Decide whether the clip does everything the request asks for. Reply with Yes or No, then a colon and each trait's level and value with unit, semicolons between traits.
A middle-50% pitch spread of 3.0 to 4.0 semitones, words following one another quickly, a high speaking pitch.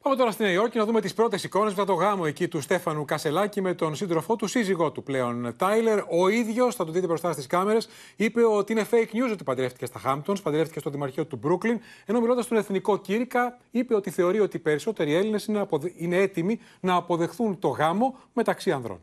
No: average, 5.2 semitones; fast, 220 wpm; high, 195 Hz